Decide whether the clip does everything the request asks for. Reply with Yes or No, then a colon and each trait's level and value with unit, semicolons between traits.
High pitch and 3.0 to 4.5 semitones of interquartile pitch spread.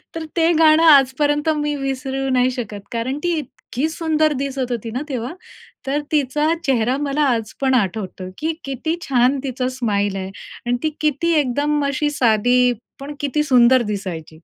Yes: very high, 265 Hz; average, 3.5 semitones